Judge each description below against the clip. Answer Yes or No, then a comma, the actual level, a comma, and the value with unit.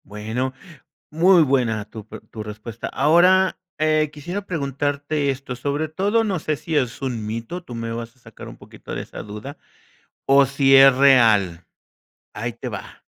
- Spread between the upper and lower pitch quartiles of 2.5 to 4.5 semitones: No, average, 5.1 semitones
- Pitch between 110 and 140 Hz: Yes, low, 135 Hz